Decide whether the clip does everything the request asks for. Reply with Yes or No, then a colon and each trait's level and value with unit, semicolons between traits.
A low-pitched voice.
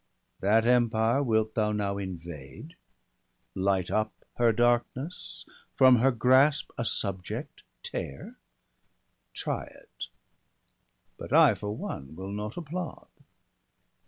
Yes: low, 110 Hz